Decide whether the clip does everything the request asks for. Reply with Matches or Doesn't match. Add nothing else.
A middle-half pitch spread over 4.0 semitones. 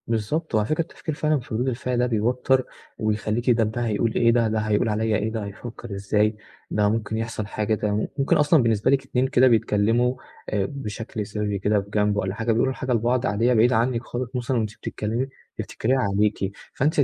Doesn't match